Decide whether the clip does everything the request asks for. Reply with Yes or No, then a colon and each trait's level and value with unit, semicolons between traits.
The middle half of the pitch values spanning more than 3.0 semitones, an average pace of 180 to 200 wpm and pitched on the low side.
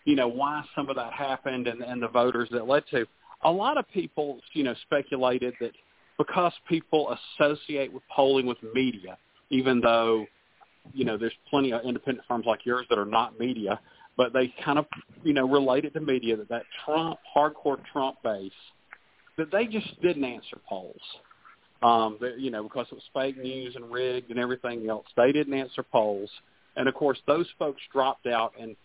Yes: average, 3.4 semitones; average, 190 wpm; low, 130 Hz